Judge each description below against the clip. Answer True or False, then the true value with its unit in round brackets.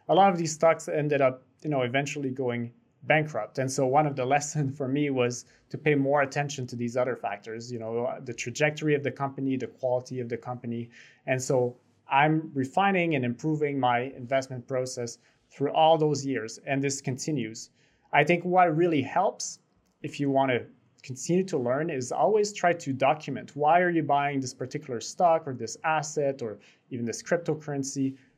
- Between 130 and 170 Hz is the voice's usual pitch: True (135 Hz)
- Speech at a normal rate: True (185 wpm)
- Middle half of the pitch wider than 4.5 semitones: False (3.3 semitones)